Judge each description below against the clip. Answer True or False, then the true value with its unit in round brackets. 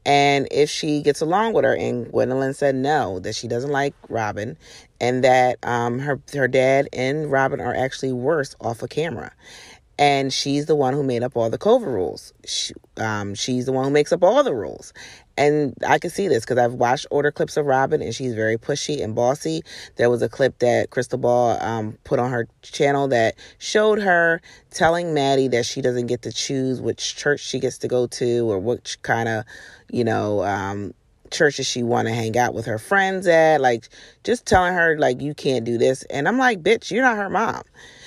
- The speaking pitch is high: False (130 Hz)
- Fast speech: True (215 wpm)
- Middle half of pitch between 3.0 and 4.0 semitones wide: True (3.5 semitones)